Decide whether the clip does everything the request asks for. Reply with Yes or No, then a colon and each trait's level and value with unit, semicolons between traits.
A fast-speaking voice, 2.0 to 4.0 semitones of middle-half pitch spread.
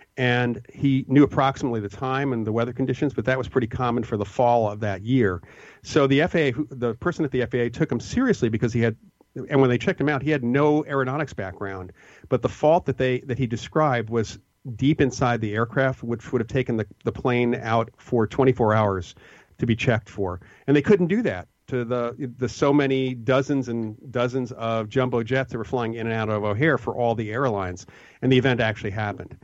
Yes: fast, 220 wpm; average, 2.9 semitones